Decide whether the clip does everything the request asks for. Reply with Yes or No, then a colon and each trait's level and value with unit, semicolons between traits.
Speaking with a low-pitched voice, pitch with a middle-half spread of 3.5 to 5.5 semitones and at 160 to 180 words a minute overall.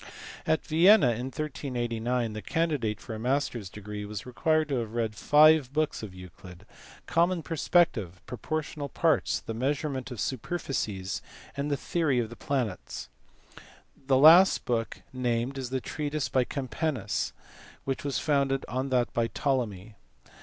No: low, 130 Hz; average, 4.8 semitones; average, 150 wpm